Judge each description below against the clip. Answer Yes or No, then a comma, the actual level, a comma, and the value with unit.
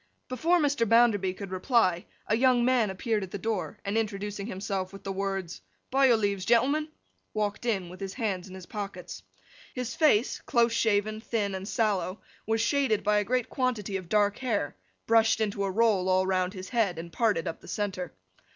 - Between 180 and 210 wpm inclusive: Yes, average, 190 wpm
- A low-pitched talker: No, high, 210 Hz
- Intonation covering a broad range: No, average, 3.4 semitones